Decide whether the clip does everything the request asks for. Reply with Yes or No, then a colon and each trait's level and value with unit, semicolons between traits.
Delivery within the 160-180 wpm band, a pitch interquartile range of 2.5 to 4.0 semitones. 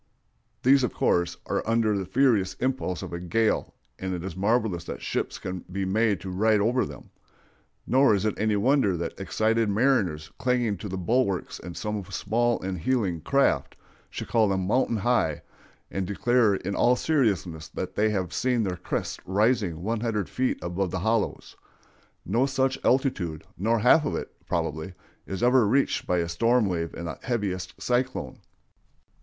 No: average, 170 wpm; average, 4.8 semitones